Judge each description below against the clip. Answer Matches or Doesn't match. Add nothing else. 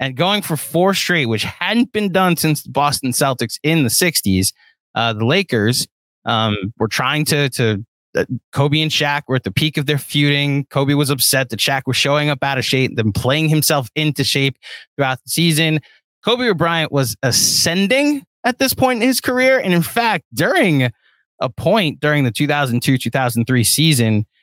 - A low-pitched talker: Doesn't match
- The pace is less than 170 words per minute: Doesn't match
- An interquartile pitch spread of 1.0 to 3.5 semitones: Doesn't match